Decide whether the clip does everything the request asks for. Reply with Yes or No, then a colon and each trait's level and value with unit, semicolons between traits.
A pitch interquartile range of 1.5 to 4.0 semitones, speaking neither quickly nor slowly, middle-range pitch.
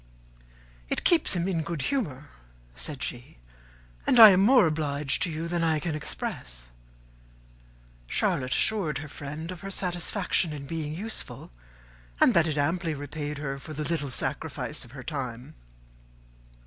Yes: average, 3.7 semitones; average, 150 wpm; medium, 155 Hz